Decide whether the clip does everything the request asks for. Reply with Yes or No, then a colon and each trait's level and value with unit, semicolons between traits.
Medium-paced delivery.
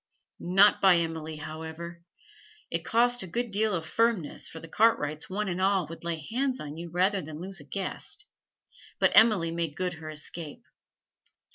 Yes: average, 170 wpm